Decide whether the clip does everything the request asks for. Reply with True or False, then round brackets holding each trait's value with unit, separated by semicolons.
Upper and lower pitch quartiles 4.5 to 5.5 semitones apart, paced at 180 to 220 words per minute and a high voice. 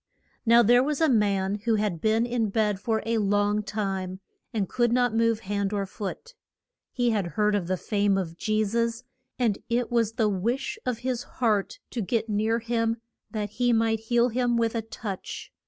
False (2.5 semitones; 190 wpm; 220 Hz)